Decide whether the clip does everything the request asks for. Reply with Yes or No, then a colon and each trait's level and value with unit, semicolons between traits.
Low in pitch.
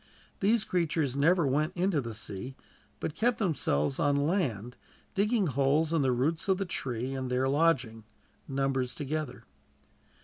No: medium, 145 Hz